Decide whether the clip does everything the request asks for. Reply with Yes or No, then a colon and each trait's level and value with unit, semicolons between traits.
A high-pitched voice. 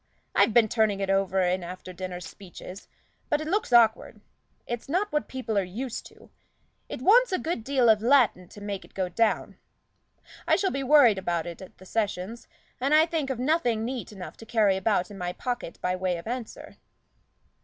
Yes: high, 220 Hz